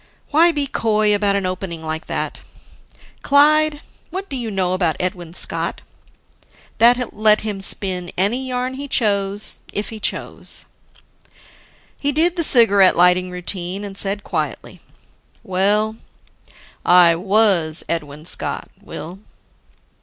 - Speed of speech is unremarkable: No, slow, 125 wpm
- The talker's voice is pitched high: Yes, high, 200 Hz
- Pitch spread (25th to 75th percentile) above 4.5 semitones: Yes, average, 5.1 semitones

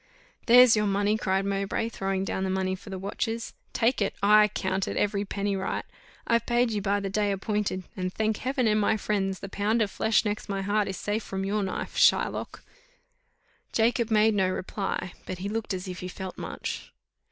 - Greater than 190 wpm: Yes, average, 200 wpm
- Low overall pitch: No, high, 205 Hz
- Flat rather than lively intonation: Yes, narrow, 2.1 semitones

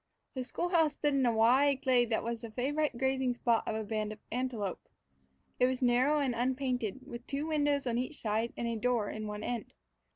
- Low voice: No, very high, 250 Hz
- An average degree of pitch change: Yes, average, 3.0 semitones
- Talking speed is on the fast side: Yes, fast, 215 wpm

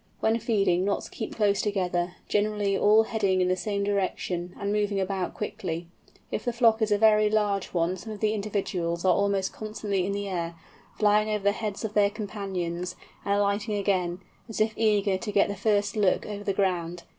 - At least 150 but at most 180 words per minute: No, average, 195 wpm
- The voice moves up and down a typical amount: No, narrow, 2.2 semitones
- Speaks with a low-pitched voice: No, high, 200 Hz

